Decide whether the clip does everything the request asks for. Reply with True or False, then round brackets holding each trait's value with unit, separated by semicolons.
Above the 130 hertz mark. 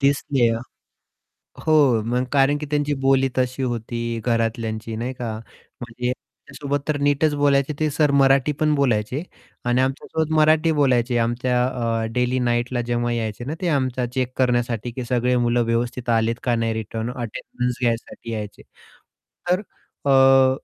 False (125 Hz)